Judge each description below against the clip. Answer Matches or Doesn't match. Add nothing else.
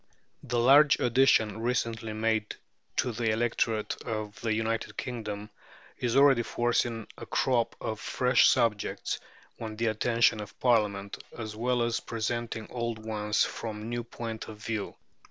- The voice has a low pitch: Matches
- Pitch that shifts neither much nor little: Doesn't match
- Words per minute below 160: Matches